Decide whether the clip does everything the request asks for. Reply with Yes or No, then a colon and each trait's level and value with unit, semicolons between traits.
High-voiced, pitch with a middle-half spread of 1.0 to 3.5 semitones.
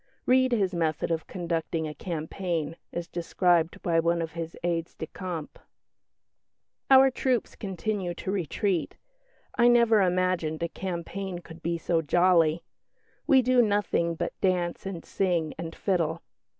No: medium, 175 Hz; average, 2.9 semitones